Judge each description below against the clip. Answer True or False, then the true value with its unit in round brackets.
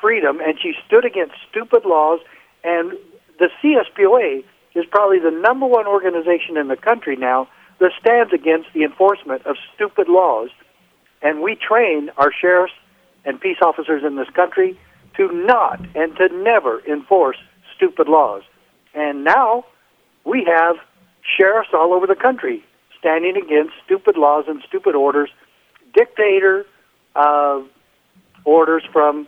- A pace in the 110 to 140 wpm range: True (135 wpm)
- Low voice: False (180 Hz)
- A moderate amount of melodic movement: False (7.4 semitones)